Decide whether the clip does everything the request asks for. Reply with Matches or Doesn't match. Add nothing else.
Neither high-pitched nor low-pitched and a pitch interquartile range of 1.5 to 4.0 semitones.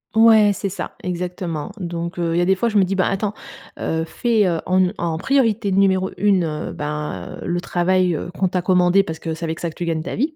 Matches